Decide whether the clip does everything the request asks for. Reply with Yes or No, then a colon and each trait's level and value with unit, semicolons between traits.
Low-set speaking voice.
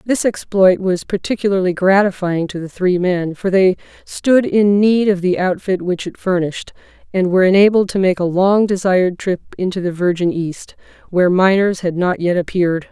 No: medium, 185 Hz